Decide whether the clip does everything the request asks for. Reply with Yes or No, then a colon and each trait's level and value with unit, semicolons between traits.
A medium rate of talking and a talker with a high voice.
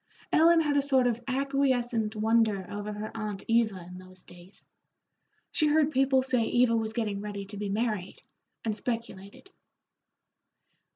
Yes: average, 150 wpm; high, 225 Hz